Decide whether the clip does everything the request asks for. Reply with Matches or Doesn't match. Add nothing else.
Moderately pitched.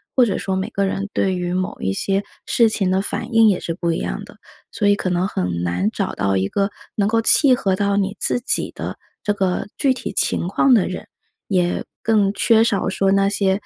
Doesn't match